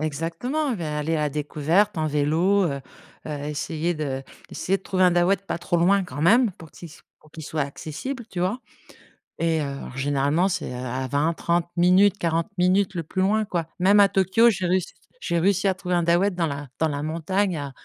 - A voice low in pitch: No, medium, 170 Hz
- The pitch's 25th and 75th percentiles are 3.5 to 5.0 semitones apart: Yes, average, 3.9 semitones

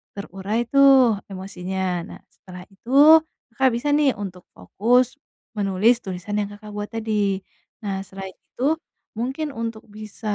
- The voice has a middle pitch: No, high, 205 Hz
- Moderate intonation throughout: Yes, average, 3.2 semitones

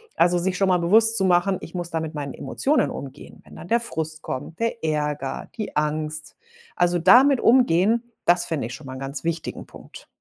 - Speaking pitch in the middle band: Yes, medium, 170 Hz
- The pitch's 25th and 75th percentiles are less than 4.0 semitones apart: No, average, 4.3 semitones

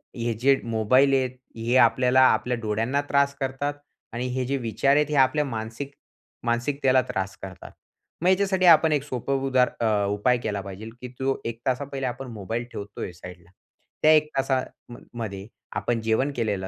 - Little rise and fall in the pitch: No, average, 3.6 semitones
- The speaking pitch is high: No, low, 125 Hz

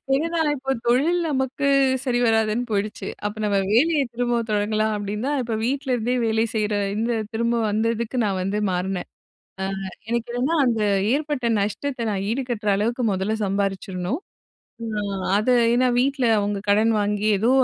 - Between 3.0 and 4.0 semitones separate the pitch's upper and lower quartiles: Yes, average, 3.5 semitones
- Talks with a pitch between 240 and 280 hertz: No, high, 230 Hz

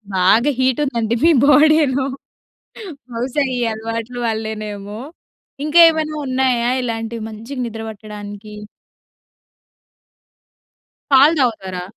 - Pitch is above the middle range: Yes, high, 230 Hz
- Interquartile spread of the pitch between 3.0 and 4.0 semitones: Yes, average, 3.5 semitones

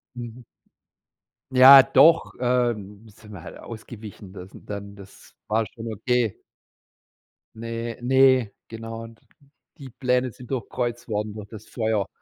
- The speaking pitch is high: No, low, 115 Hz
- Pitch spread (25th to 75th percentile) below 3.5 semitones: Yes, average, 2.8 semitones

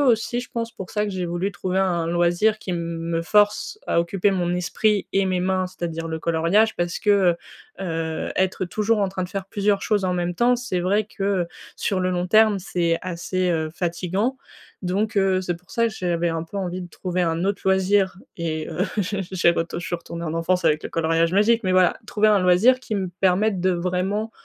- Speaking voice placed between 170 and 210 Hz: Yes, medium, 185 Hz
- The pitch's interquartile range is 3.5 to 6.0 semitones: No, average, 2.8 semitones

